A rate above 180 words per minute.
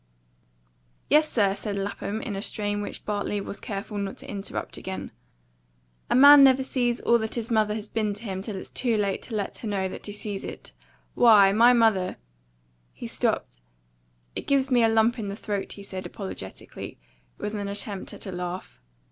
Yes: average, 195 wpm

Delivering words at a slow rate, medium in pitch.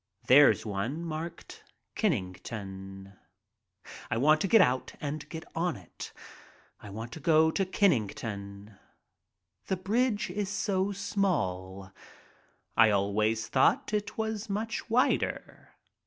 Yes: slow, 125 wpm; medium, 150 Hz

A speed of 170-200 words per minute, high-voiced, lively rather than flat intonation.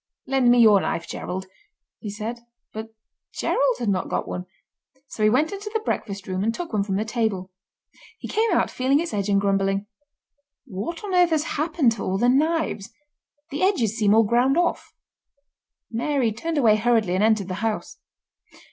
Yes: average, 180 wpm; high, 230 Hz; wide, 6.6 semitones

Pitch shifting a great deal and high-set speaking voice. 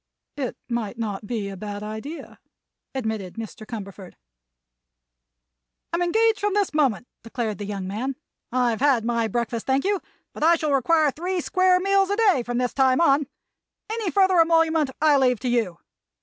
Yes: wide, 7.0 semitones; very high, 260 Hz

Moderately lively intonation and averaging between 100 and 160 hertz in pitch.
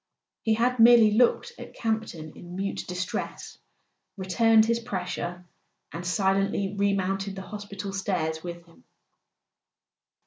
No: average, 3.4 semitones; high, 195 Hz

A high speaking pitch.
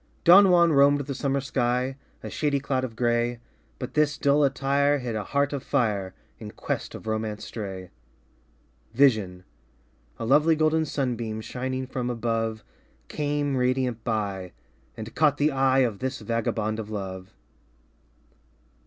No: low, 130 Hz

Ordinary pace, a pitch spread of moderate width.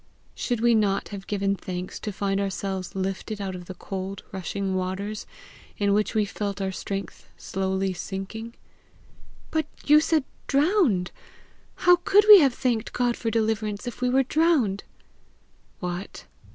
Yes: average, 150 wpm; average, 4.0 semitones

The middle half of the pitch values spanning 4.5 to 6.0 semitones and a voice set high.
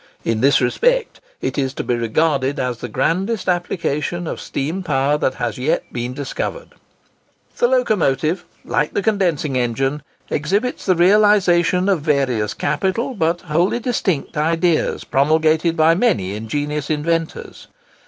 No: average, 5.3 semitones; medium, 155 Hz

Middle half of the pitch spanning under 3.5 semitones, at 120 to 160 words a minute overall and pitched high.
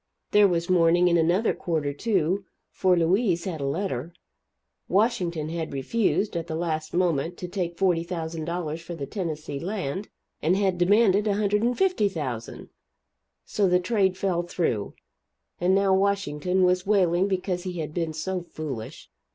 No: average, 3.1 semitones; average, 145 wpm; medium, 175 Hz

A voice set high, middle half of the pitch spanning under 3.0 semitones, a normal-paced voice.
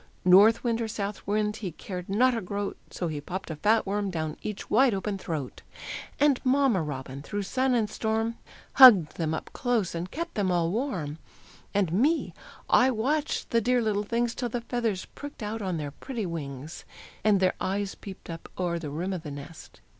No: high, 205 Hz; average, 5.3 semitones; average, 195 wpm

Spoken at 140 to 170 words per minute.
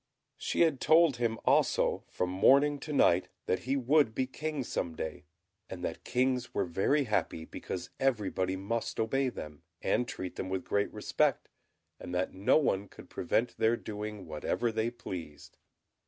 Yes: average, 165 wpm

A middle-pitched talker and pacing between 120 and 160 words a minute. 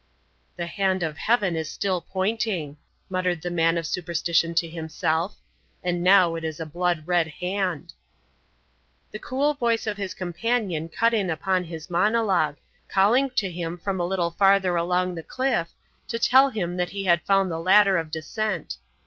No: medium, 180 Hz; average, 170 wpm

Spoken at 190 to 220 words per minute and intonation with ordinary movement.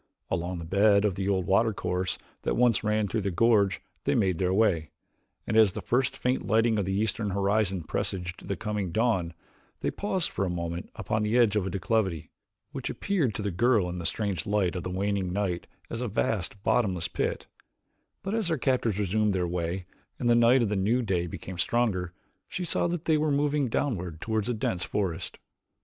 Yes: average, 200 wpm; average, 4.1 semitones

